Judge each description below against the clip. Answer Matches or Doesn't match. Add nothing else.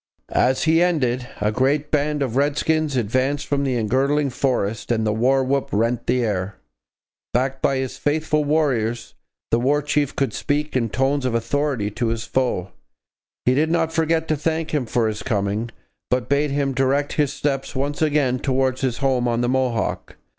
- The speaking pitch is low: Matches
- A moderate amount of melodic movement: Matches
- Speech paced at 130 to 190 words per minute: Matches